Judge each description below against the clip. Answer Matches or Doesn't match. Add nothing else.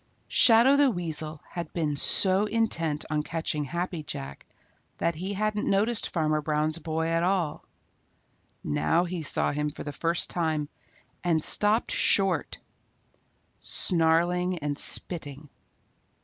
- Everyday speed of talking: Doesn't match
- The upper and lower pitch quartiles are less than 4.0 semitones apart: Matches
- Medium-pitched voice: Matches